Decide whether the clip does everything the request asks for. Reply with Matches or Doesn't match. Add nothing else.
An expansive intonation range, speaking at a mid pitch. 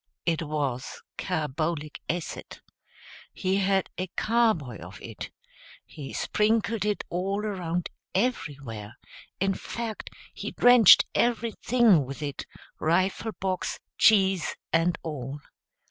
Matches